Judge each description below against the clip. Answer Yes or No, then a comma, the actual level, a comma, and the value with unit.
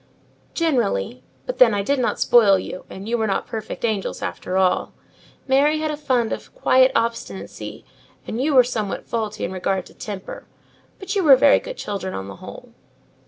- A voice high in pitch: Yes, high, 230 Hz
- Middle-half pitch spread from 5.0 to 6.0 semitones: Yes, wide, 5.5 semitones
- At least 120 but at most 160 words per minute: No, average, 185 wpm